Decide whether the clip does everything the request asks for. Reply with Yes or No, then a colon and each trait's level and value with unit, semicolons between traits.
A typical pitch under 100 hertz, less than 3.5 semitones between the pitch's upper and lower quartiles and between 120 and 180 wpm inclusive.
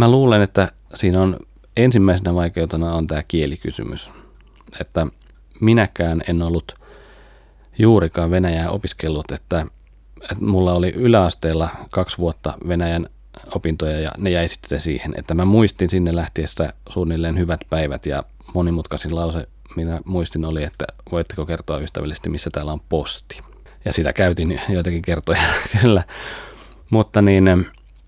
Yes: very low, 85 Hz; narrow, 2.6 semitones; average, 135 wpm